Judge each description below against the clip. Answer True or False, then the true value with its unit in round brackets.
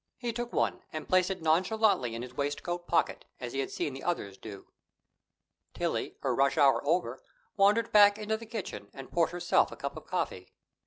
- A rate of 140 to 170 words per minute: False (195 wpm)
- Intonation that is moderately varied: False (7.3 semitones)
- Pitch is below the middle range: False (175 Hz)